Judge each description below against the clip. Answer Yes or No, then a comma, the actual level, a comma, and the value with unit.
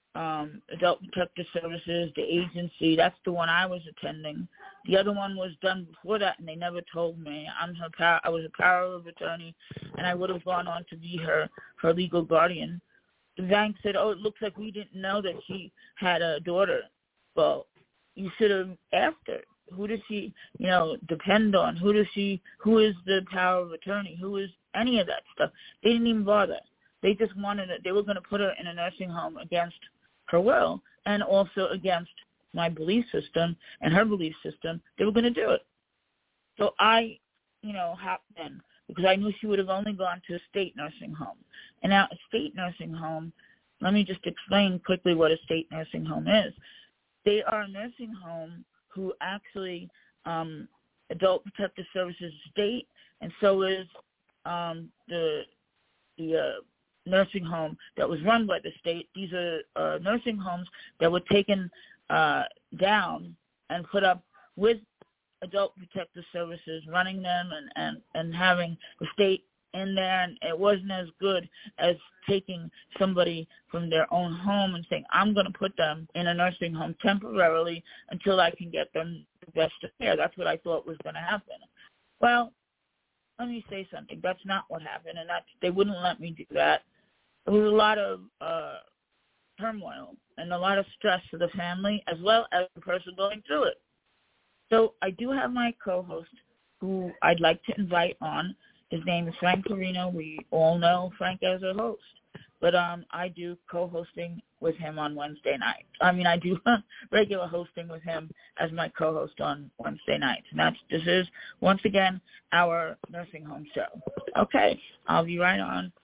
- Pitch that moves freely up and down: No, average, 3.0 semitones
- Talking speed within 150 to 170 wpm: No, average, 185 wpm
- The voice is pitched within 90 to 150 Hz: No, medium, 180 Hz